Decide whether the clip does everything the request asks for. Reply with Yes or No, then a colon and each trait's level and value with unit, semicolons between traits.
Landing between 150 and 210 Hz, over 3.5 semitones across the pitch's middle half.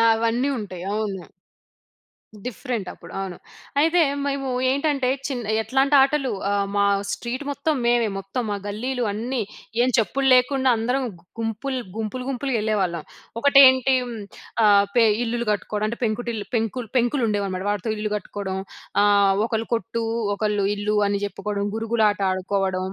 No: high, 225 Hz; average, 4.1 semitones